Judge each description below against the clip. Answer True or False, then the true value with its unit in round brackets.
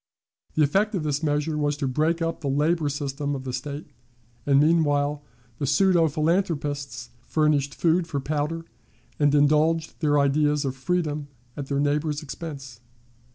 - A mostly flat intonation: True (2.0 semitones)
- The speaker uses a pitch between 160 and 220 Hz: False (145 Hz)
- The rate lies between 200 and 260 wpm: False (155 wpm)